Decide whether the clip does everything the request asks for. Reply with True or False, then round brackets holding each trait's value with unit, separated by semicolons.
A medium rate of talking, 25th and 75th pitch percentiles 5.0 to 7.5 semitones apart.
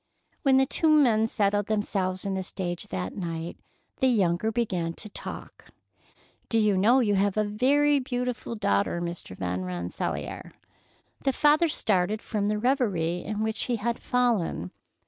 True (155 wpm; 5.5 semitones)